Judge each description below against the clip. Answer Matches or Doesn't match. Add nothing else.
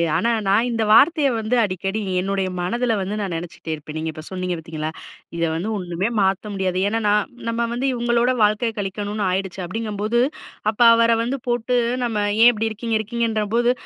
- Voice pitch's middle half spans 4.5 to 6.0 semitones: Doesn't match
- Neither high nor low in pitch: Doesn't match